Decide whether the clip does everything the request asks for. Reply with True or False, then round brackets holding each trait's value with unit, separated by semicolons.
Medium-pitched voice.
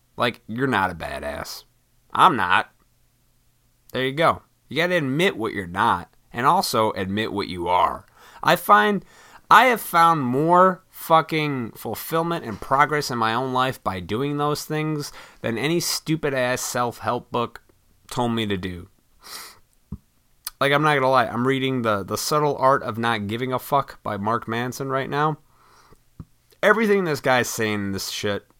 False (130 Hz)